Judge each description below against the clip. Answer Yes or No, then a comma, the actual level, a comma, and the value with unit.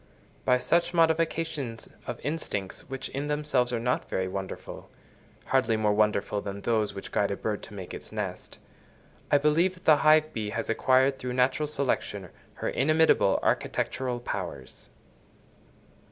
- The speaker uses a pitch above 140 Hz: No, low, 125 Hz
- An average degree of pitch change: No, wide, 5.8 semitones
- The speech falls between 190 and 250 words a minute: No, average, 140 wpm